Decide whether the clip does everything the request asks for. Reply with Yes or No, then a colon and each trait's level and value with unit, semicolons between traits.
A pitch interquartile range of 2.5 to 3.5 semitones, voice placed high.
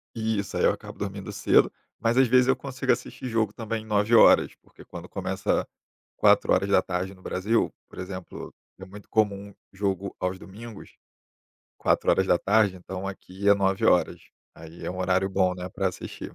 No: average, 3.1 semitones; low, 100 Hz